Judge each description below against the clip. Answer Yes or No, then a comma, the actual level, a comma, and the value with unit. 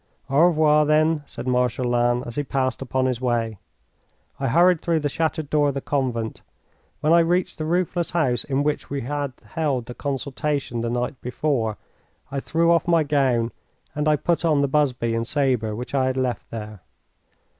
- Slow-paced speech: No, average, 190 wpm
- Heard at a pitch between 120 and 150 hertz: Yes, medium, 140 Hz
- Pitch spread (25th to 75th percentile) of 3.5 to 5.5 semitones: Yes, average, 3.9 semitones